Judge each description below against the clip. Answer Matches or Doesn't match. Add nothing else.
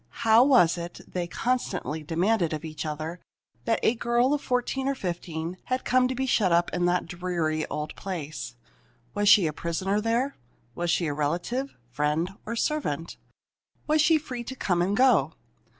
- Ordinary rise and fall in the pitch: Doesn't match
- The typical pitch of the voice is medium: Matches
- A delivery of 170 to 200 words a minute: Matches